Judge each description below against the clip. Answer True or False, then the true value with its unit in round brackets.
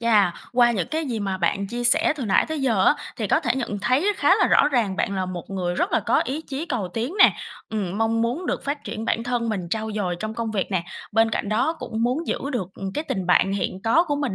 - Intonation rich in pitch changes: False (4.7 semitones)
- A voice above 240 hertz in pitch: False (225 Hz)